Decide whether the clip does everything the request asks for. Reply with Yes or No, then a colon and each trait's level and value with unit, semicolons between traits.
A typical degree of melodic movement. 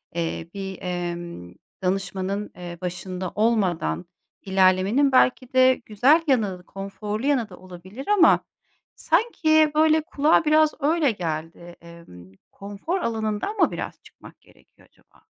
No: wide, 7.7 semitones